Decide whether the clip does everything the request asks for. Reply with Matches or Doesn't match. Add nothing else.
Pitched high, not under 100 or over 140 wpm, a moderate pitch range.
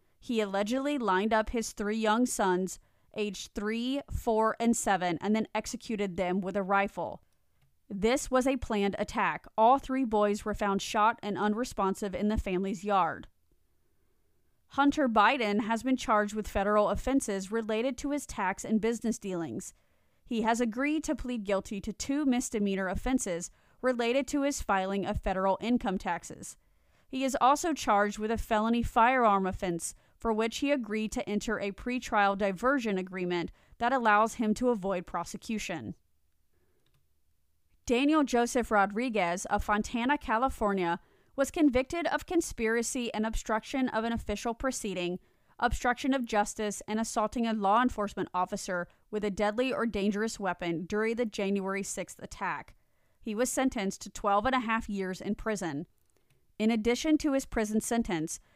Doesn't match